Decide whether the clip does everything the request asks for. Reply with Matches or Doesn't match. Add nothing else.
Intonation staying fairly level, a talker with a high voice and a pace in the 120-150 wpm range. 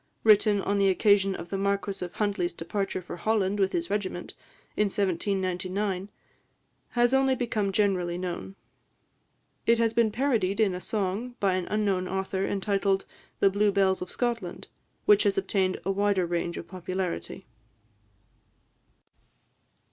Matches